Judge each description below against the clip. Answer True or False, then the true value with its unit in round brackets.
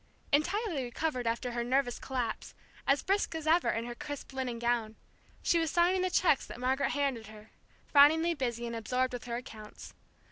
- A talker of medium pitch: False (255 Hz)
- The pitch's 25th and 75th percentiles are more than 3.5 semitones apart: True (4.7 semitones)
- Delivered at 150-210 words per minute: True (180 wpm)